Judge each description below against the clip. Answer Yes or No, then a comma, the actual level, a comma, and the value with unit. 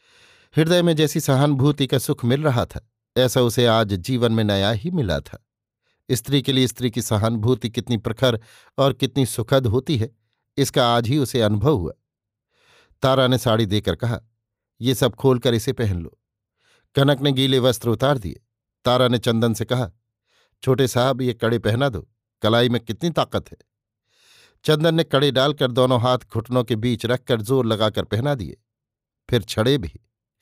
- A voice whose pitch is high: No, low, 125 Hz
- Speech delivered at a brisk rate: No, average, 170 wpm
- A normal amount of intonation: Yes, average, 3.1 semitones